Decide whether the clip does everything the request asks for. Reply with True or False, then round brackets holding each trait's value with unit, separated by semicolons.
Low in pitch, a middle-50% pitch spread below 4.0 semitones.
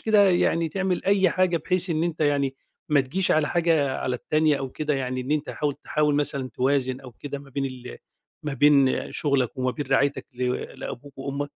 False (145 Hz; 2.9 semitones)